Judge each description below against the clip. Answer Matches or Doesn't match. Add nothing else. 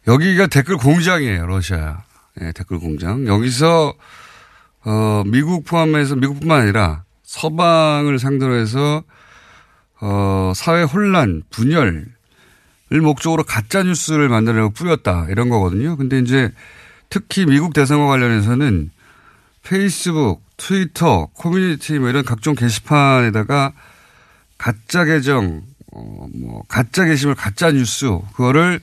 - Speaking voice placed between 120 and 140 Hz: Matches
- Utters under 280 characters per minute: Matches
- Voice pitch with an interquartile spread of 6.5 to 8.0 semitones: Matches